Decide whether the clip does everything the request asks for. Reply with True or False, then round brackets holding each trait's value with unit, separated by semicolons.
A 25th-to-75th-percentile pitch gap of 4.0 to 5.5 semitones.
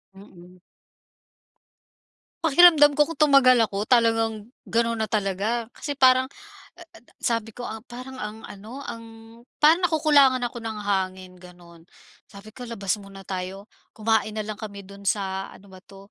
True (4.5 semitones)